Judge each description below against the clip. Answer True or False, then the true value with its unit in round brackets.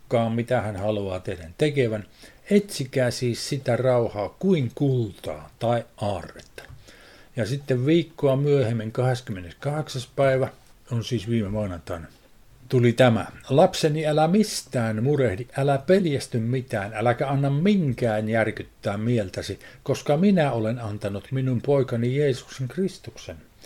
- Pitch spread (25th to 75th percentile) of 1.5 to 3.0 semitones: False (4.3 semitones)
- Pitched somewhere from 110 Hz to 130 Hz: True (125 Hz)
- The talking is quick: False (115 wpm)